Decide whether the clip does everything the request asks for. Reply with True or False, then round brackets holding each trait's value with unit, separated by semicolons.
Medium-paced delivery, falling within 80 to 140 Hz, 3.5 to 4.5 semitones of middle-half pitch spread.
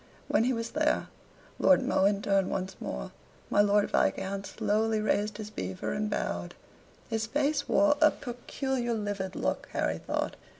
False (155 wpm; 215 Hz; 4.0 semitones)